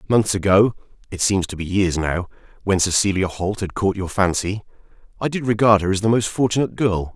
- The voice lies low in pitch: Yes, low, 100 Hz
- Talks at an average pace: Yes, average, 185 wpm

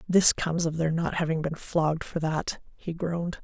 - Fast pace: Yes, fast, 210 wpm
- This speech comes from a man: No, female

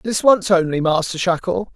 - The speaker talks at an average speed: Yes, average, 170 wpm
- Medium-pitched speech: Yes, medium, 180 Hz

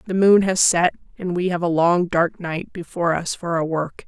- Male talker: No, female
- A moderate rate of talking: No, fast, 235 wpm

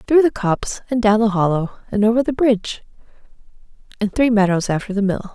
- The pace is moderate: Yes, average, 190 wpm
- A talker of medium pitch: No, high, 215 Hz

